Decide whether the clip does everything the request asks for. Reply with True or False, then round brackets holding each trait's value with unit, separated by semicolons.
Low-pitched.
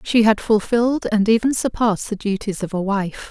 False (215 Hz)